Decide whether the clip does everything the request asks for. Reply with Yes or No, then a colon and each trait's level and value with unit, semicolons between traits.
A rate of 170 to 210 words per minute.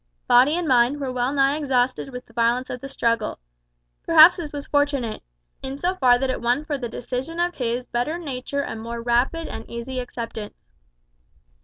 Yes: average, 185 wpm